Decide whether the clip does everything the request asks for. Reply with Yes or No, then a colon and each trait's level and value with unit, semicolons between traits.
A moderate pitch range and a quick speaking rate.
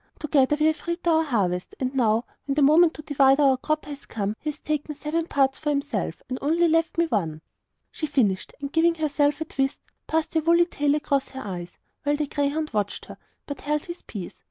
Yes: average, 3.0 semitones; fast, 220 wpm